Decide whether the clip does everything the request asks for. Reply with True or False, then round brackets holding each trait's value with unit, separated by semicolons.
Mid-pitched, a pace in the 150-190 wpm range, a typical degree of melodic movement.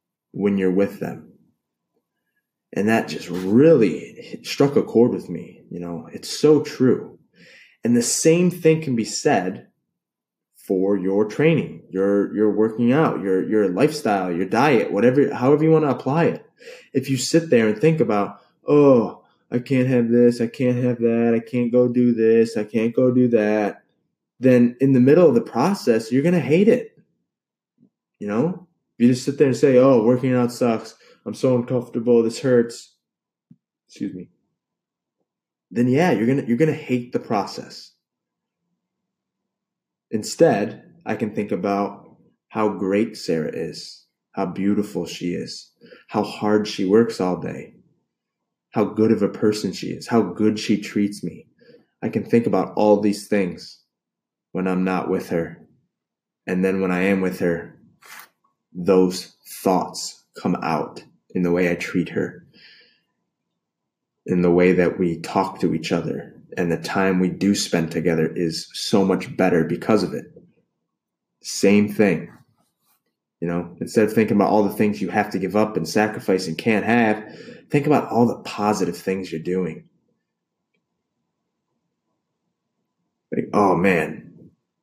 False (110 Hz; 160 wpm; 4.7 semitones)